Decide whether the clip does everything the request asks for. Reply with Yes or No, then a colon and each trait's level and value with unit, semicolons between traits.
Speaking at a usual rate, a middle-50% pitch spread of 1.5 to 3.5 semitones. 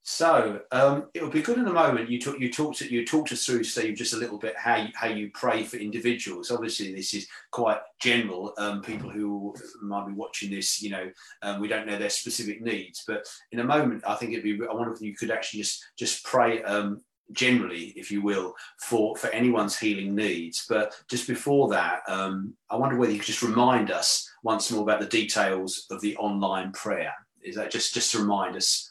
No: fast, 220 wpm; average, 2.8 semitones